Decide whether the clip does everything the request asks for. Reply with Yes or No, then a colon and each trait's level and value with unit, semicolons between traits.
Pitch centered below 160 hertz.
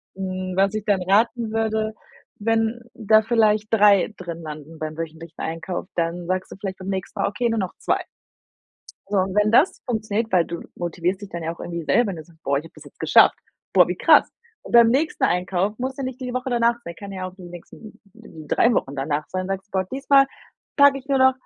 No: high, 195 Hz